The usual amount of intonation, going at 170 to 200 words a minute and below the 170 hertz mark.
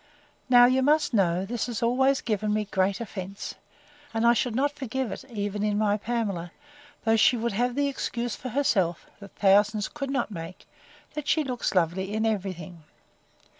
No: average, 4.0 semitones; average, 180 wpm; high, 220 Hz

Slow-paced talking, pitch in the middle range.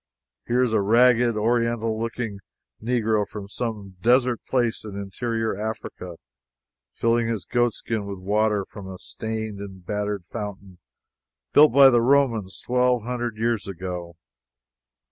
No: slow, 130 wpm; low, 110 Hz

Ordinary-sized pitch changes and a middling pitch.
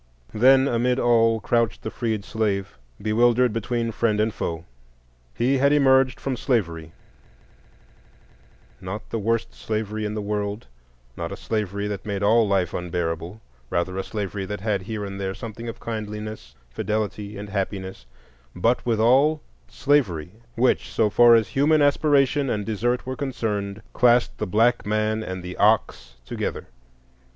No: average, 3.3 semitones; low, 110 Hz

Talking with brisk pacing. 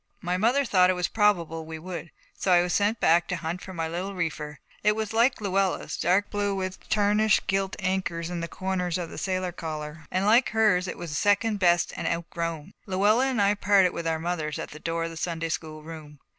Yes: fast, 220 wpm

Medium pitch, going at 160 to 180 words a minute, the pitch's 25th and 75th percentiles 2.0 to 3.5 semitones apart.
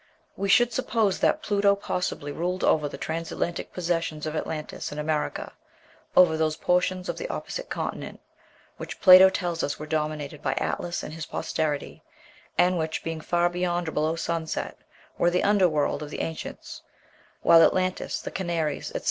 Yes: medium, 165 Hz; average, 170 wpm; average, 2.7 semitones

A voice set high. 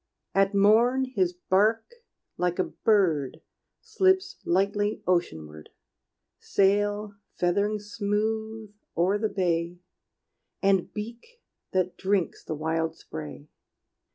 Yes: high, 200 Hz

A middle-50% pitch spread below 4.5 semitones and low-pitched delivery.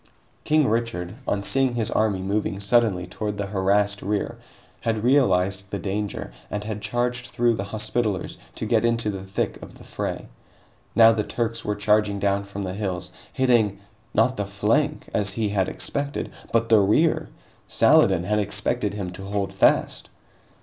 Yes: average, 2.8 semitones; low, 105 Hz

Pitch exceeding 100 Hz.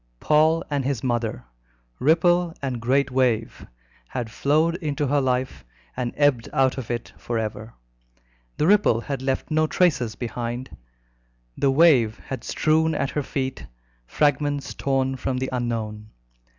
Yes: low, 135 Hz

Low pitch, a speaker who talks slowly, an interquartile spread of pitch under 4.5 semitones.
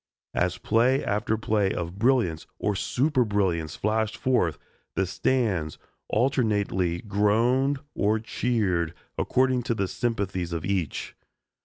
No: low, 105 Hz; slow, 115 wpm; average, 4.8 semitones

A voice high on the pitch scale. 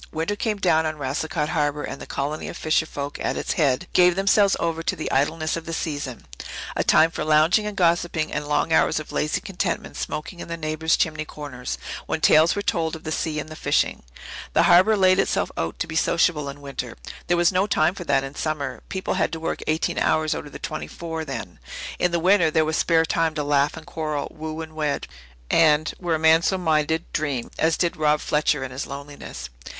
No: medium, 160 Hz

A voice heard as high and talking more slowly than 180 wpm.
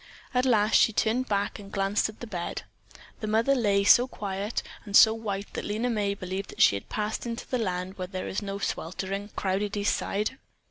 No: high, 205 Hz; fast, 205 wpm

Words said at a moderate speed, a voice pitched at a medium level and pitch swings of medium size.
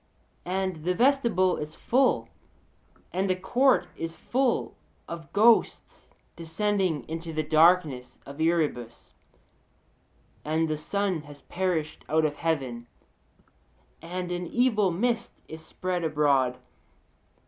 No: slow, 115 wpm; medium, 170 Hz; average, 3.9 semitones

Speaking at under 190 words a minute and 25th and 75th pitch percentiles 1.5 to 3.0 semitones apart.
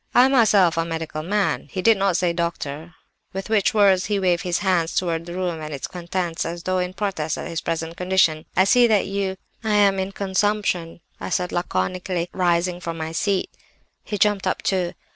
No: average, 200 wpm; average, 2.7 semitones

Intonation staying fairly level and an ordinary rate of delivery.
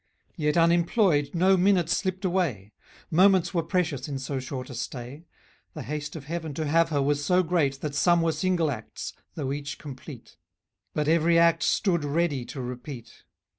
No: average, 3.6 semitones; average, 180 wpm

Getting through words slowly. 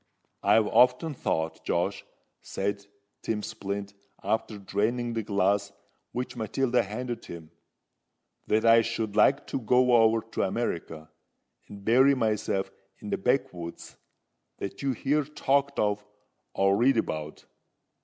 Yes: slow, 125 wpm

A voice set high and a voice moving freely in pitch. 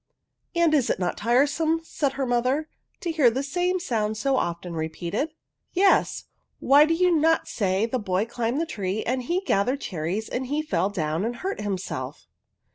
Yes: very high, 250 Hz; wide, 7.5 semitones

